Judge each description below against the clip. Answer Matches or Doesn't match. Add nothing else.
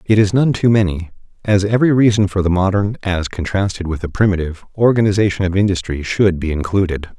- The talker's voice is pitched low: Matches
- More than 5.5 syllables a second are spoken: Matches